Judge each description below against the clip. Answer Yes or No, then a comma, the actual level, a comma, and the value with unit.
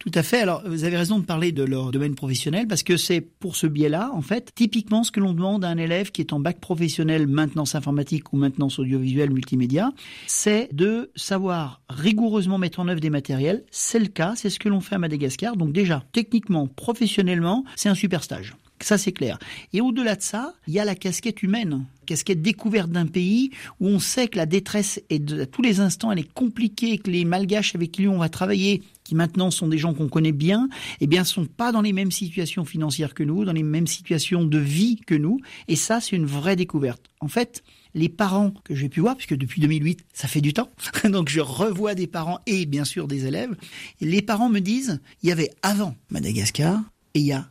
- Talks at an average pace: No, fast, 230 wpm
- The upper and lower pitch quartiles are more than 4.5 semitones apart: Yes, average, 5.1 semitones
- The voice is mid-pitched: Yes, medium, 180 Hz